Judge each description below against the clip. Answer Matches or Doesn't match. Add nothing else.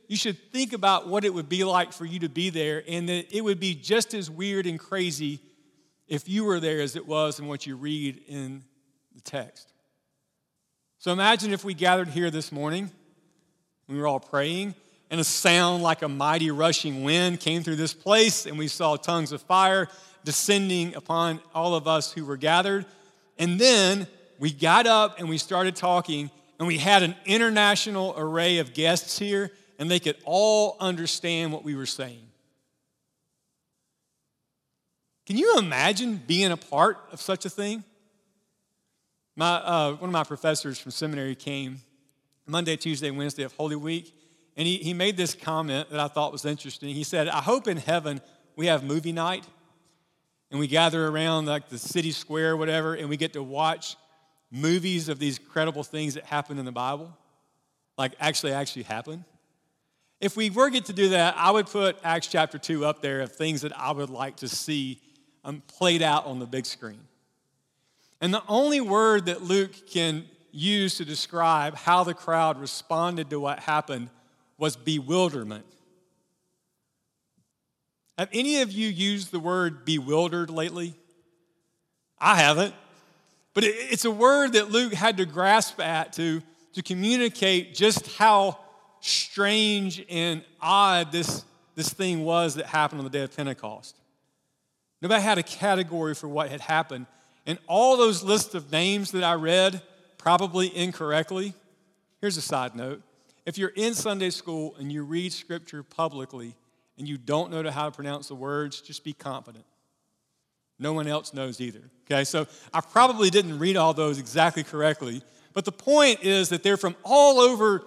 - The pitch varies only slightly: Doesn't match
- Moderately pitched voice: Matches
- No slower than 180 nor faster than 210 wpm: Doesn't match